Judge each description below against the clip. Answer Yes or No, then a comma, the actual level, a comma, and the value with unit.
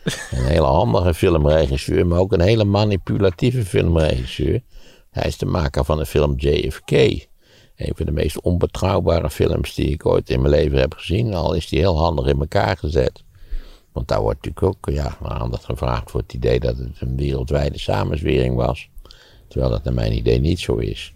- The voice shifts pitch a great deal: Yes, wide, 5.8 semitones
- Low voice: Yes, very low, 75 Hz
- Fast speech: No, average, 185 wpm